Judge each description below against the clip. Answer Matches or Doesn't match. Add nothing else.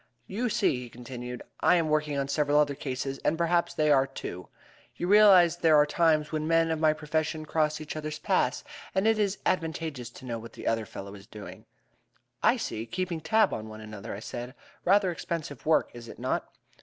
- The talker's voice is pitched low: Doesn't match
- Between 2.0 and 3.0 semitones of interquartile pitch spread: Doesn't match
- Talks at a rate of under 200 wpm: Doesn't match